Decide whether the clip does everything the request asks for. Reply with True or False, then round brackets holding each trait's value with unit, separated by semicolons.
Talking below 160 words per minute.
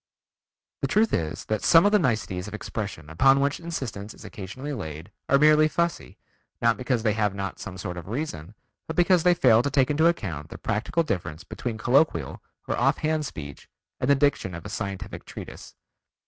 False (190 wpm)